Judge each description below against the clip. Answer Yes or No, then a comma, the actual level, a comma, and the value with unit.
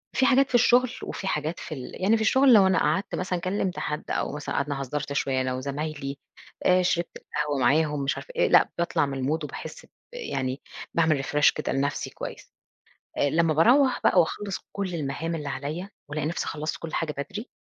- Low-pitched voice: No, medium, 160 Hz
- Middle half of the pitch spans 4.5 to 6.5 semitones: Yes, average, 4.9 semitones